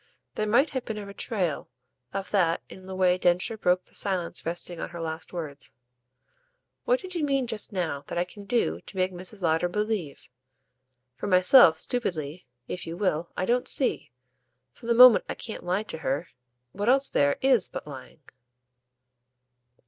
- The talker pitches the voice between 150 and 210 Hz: Yes, medium, 185 Hz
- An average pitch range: Yes, average, 4.7 semitones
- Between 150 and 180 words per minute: Yes, average, 175 wpm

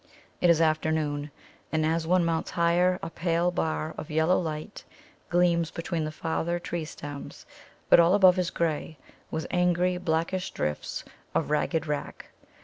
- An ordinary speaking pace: Yes, average, 150 wpm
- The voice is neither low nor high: Yes, medium, 165 Hz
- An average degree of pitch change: No, narrow, 1.9 semitones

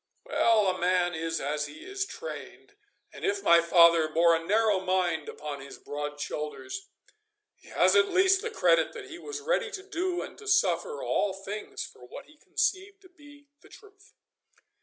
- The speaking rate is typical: Yes, average, 180 wpm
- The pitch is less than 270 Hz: No, very high, 280 Hz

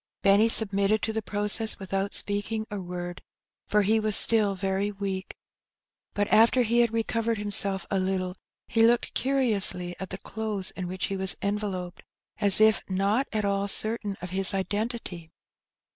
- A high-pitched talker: Yes, high, 205 Hz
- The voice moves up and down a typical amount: No, narrow, 2.3 semitones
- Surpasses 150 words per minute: Yes, average, 165 wpm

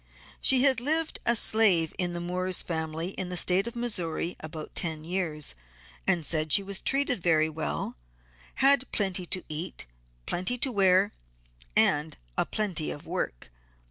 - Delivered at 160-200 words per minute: No, average, 150 wpm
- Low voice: No, medium, 180 Hz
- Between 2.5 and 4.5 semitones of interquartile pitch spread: No, average, 5.1 semitones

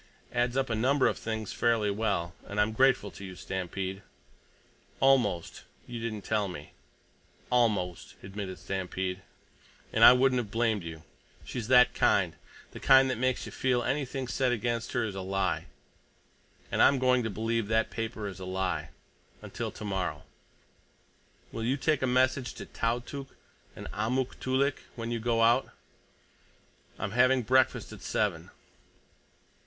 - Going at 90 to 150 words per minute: Yes, average, 145 wpm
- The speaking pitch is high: No, low, 115 Hz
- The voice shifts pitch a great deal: No, average, 4.3 semitones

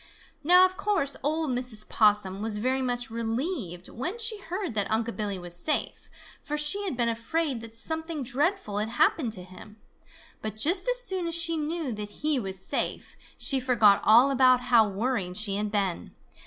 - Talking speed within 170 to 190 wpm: Yes, average, 180 wpm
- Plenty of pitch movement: Yes, wide, 7.0 semitones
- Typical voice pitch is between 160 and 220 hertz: No, high, 245 Hz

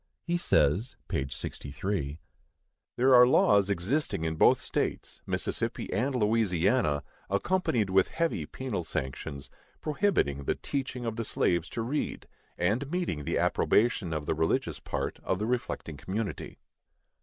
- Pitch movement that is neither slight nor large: No, wide, 7.7 semitones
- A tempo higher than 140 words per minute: No, slow, 135 wpm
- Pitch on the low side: Yes, low, 100 Hz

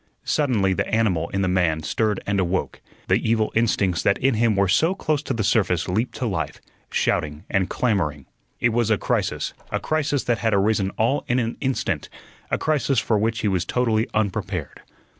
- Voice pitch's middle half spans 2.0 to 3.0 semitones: No, average, 4.0 semitones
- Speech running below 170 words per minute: No, average, 190 wpm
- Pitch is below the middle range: Yes, low, 110 Hz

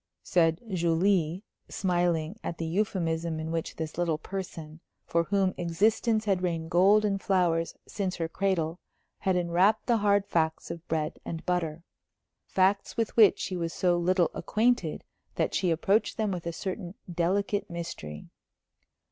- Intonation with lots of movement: No, average, 3.0 semitones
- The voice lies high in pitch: No, medium, 175 Hz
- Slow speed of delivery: No, average, 150 wpm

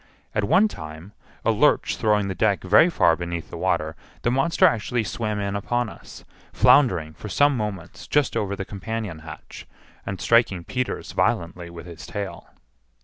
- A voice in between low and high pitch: No, low, 100 Hz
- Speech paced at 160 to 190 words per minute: Yes, average, 165 wpm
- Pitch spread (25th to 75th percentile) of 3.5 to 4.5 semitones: No, average, 5.1 semitones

